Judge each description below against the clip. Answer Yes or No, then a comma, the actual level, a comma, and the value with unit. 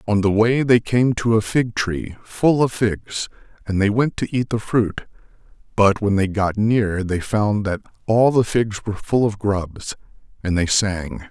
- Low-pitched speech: Yes, low, 105 Hz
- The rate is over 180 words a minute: Yes, average, 195 wpm